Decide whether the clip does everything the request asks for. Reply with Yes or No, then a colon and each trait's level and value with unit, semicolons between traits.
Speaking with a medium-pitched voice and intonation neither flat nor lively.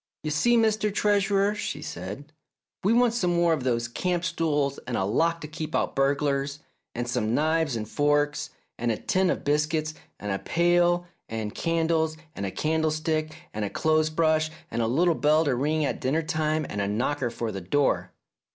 Yes: medium, 155 Hz; average, 4.4 semitones